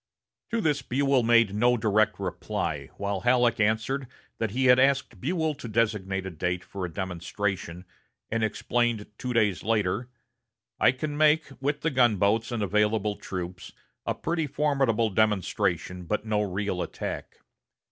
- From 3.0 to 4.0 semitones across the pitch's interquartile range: No, average, 4.4 semitones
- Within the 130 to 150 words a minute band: Yes, average, 145 wpm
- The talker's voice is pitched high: No, low, 110 Hz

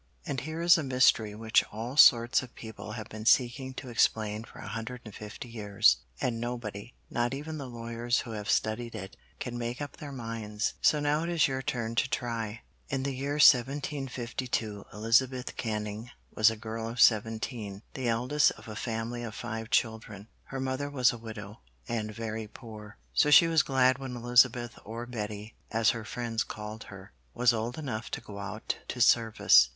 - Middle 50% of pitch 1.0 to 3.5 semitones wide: Yes, average, 2.8 semitones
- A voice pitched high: No, low, 115 Hz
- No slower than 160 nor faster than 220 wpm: Yes, average, 185 wpm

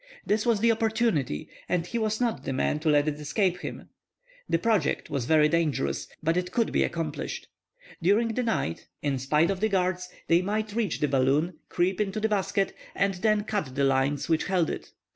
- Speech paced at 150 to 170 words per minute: No, average, 200 wpm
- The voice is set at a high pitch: No, medium, 180 Hz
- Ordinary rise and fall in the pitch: No, wide, 6.1 semitones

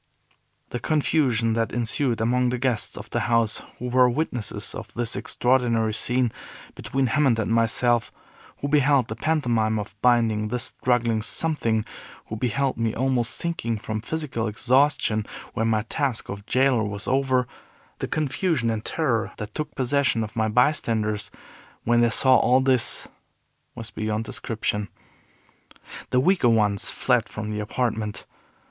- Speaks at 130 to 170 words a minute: Yes, average, 145 wpm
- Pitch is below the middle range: Yes, low, 120 Hz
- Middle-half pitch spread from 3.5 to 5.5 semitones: No, average, 2.8 semitones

